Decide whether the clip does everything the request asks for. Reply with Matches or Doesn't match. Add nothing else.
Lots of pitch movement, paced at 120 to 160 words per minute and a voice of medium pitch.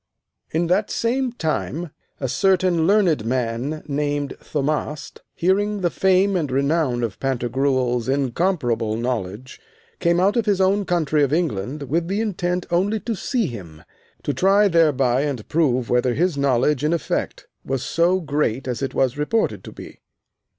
Matches